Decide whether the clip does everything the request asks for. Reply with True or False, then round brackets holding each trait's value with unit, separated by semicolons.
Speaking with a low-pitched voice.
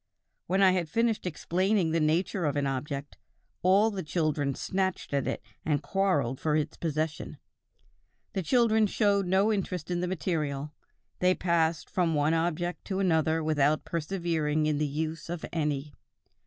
False (165 Hz)